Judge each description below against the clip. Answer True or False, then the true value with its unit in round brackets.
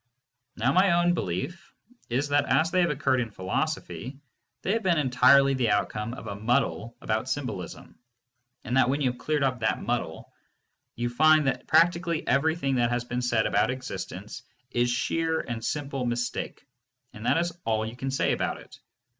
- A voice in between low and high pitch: False (130 Hz)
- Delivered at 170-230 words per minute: True (180 wpm)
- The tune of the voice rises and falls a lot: False (4.6 semitones)